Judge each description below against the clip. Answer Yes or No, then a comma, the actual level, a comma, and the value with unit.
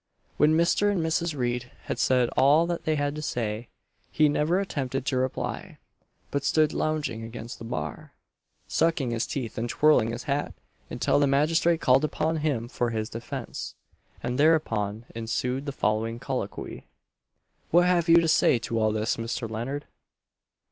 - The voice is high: No, low, 135 Hz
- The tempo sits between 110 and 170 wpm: Yes, average, 160 wpm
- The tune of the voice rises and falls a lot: No, average, 5.0 semitones